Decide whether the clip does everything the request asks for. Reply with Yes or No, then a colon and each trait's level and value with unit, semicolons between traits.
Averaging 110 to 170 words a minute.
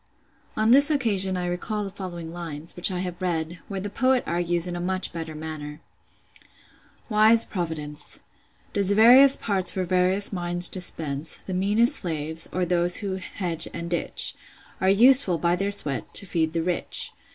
Yes: average, 165 wpm